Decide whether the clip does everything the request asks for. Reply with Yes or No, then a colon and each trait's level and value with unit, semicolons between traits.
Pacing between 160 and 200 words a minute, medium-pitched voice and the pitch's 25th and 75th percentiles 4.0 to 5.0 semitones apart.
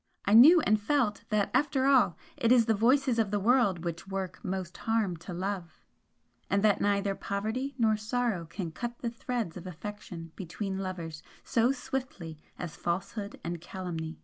No: average, 170 wpm; high, 200 Hz; average, 4.7 semitones